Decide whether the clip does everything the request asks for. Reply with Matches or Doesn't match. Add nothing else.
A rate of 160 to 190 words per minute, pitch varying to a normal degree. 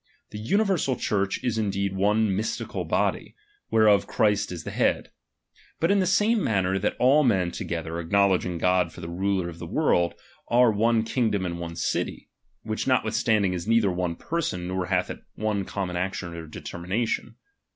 Matches